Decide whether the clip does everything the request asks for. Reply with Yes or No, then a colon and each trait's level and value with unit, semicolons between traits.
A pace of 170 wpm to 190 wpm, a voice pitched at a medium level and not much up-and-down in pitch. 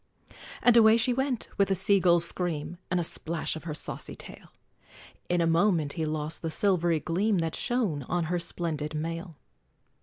No: average, 180 wpm; medium, 170 Hz; average, 3.6 semitones